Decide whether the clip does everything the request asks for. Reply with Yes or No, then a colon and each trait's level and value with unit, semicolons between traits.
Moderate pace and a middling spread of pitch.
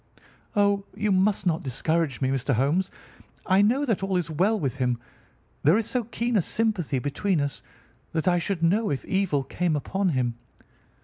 No: average, 180 wpm; wide, 6.0 semitones